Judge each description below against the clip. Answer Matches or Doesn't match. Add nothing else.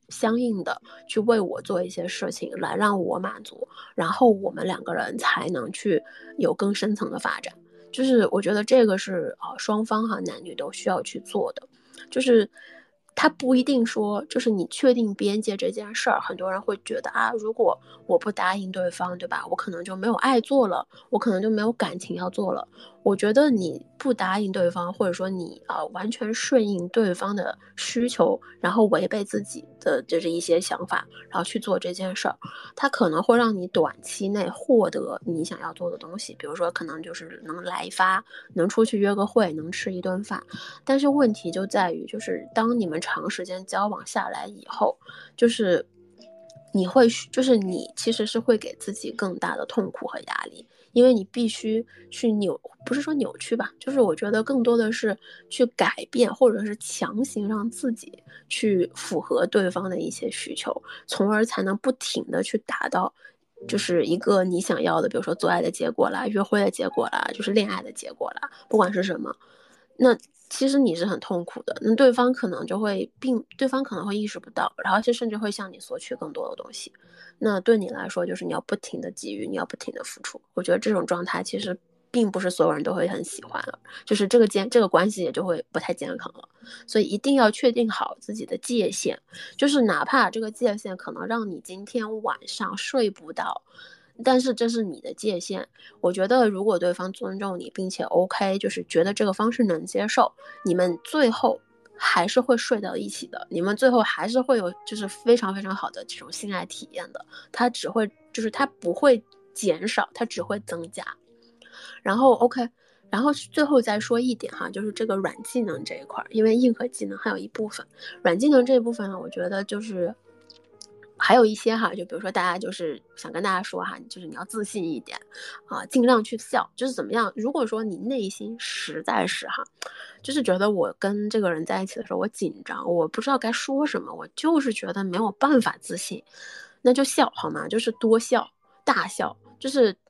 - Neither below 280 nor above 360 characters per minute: Matches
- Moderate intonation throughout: Matches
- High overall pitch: Matches